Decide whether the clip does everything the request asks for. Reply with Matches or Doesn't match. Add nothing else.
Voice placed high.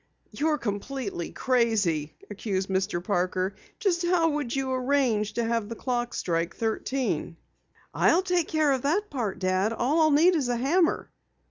Matches